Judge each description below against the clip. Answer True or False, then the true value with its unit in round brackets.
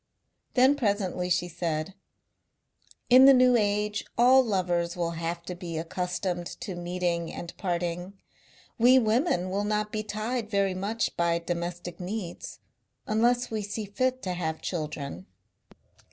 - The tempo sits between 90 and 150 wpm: True (140 wpm)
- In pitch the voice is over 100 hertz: True (185 Hz)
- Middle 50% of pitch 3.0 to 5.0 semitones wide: True (4.1 semitones)